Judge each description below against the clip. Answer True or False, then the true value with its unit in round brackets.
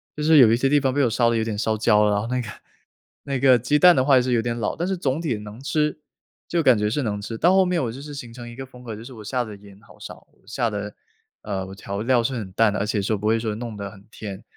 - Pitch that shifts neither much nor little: True (4.0 semitones)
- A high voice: False (120 Hz)